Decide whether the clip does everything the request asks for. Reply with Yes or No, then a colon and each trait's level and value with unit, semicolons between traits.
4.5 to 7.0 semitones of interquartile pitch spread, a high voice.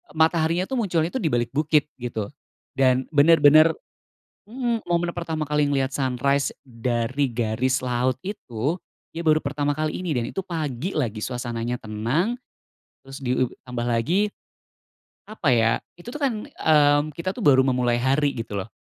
No: average, 5.1 semitones; medium, 140 Hz